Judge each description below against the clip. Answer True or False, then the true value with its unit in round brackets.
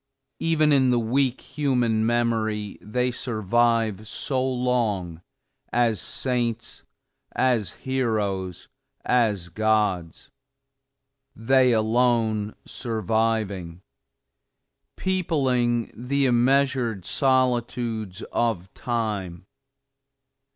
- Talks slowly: True (75 wpm)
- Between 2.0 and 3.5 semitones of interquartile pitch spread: True (2.8 semitones)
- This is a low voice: True (115 Hz)